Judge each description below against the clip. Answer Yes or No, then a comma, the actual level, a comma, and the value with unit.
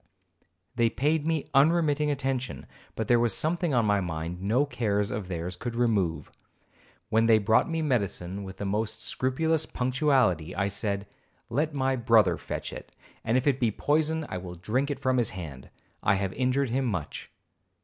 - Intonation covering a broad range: Yes, wide, 5.7 semitones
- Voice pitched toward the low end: Yes, low, 115 Hz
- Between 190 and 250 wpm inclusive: No, average, 175 wpm